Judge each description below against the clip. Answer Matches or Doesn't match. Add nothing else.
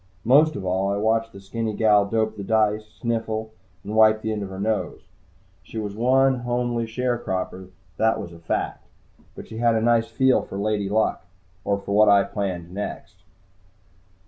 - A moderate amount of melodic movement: Doesn't match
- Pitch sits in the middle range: Doesn't match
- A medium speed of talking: Matches